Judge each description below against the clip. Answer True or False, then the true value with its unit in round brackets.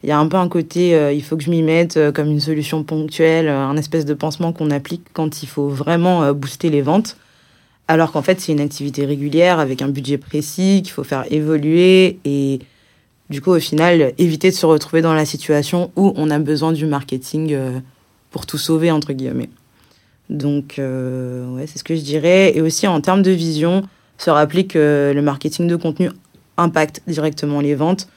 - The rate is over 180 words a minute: True (210 wpm)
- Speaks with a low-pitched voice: False (155 Hz)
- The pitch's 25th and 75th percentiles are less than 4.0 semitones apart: True (2.8 semitones)